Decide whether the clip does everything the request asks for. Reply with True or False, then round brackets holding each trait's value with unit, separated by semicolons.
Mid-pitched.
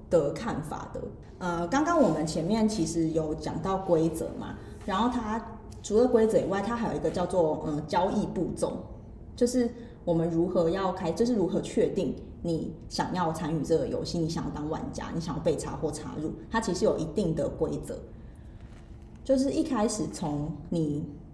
True (175 Hz)